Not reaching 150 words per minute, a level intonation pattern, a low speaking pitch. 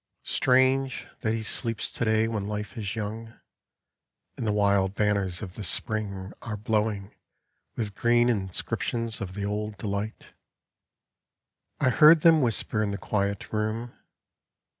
Yes: average, 140 wpm; narrow, 2.3 semitones; low, 105 Hz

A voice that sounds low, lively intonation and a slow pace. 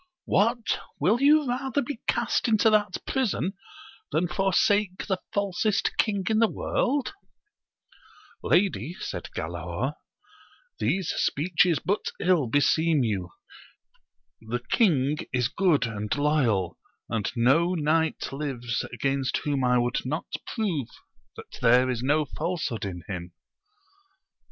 No: medium, 155 Hz; wide, 8.2 semitones; slow, 125 wpm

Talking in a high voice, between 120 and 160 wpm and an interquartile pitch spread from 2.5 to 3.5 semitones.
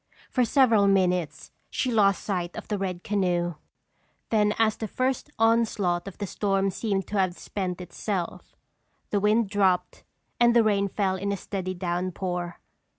Yes: high, 195 Hz; average, 155 wpm; average, 2.9 semitones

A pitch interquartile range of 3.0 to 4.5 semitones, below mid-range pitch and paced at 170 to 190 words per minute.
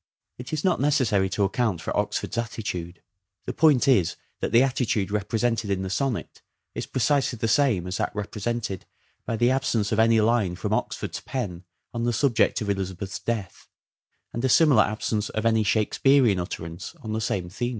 Yes: average, 3.8 semitones; low, 110 Hz; average, 180 wpm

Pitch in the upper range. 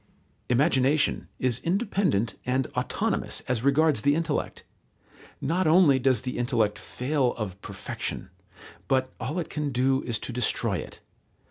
No: low, 135 Hz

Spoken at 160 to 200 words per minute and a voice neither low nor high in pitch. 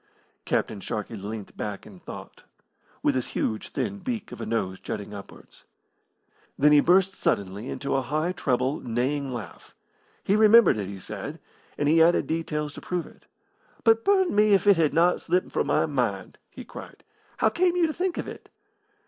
Yes: average, 180 wpm; medium, 150 Hz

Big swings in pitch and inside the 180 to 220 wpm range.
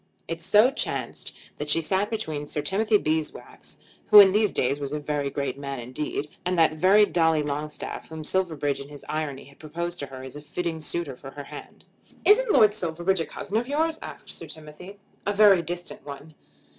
No: average, 4.8 semitones; average, 195 wpm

